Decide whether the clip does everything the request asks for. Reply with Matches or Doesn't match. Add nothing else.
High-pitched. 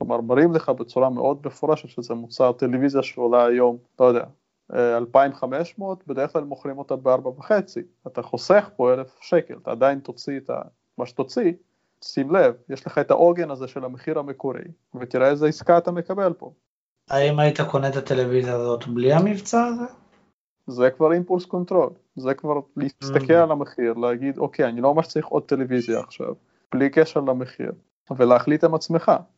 Doesn't match